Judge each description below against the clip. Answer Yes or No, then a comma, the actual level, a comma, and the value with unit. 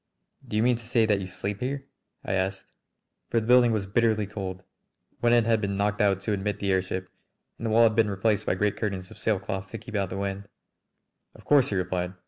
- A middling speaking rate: No, fast, 230 wpm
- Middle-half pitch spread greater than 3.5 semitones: No, average, 2.8 semitones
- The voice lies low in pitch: Yes, low, 105 Hz